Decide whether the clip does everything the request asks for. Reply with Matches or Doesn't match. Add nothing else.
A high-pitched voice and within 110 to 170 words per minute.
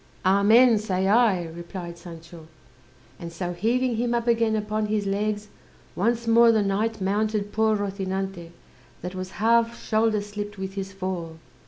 Matches